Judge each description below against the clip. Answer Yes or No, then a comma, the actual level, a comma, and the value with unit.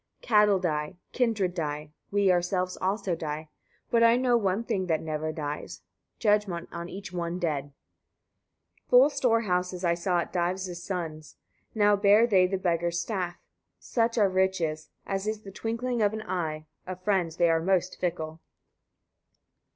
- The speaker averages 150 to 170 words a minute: Yes, average, 160 wpm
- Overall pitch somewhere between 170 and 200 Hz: Yes, medium, 185 Hz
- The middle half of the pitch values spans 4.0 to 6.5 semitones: No, average, 3.4 semitones